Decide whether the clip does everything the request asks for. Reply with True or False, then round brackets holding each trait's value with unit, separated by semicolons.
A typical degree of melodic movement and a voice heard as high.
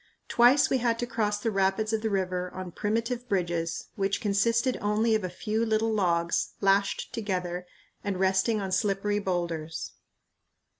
True (3.3 semitones; 205 Hz)